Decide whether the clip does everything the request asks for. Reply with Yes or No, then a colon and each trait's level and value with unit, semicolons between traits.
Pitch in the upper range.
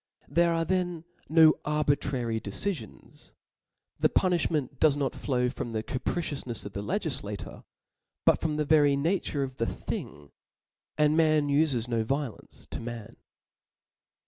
No: medium, 145 Hz